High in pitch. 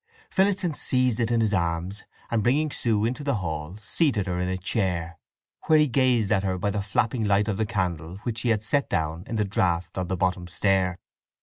No: low, 105 Hz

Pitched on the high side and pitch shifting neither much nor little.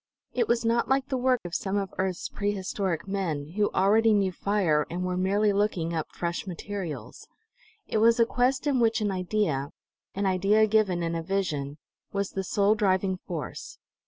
Yes: high, 195 Hz; average, 3.2 semitones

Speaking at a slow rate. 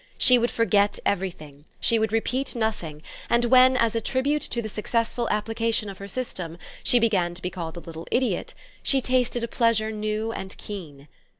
No: average, 185 wpm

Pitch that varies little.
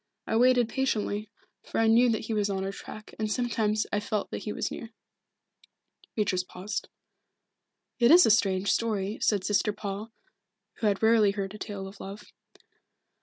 Yes: narrow, 2.1 semitones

